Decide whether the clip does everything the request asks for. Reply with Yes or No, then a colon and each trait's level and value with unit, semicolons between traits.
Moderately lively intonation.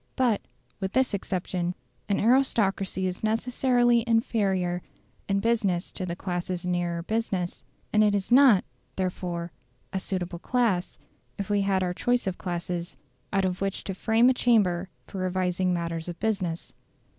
Yes: average, 3.8 semitones